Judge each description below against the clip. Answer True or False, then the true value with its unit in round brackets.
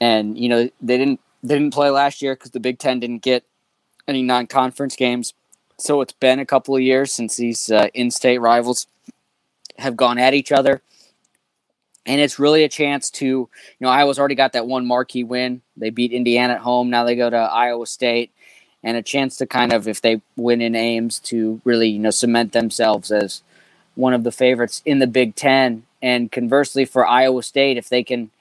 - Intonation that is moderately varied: False (2.1 semitones)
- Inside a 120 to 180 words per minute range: False (205 wpm)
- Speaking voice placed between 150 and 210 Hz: False (125 Hz)